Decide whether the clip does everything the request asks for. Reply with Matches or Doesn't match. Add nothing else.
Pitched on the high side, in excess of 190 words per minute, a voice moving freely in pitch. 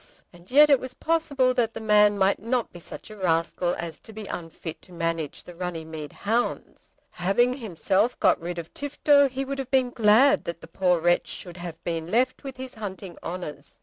Matches